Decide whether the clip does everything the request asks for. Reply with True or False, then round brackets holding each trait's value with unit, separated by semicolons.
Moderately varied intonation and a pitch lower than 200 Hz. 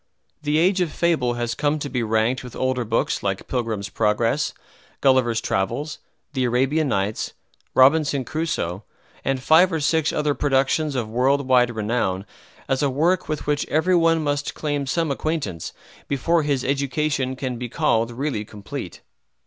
True (4.1 semitones; 135 Hz)